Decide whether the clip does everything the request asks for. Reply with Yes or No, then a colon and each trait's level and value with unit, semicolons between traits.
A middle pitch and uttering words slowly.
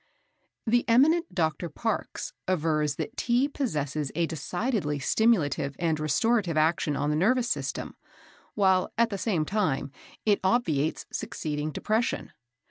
Yes: medium, 175 Hz; slow, 130 wpm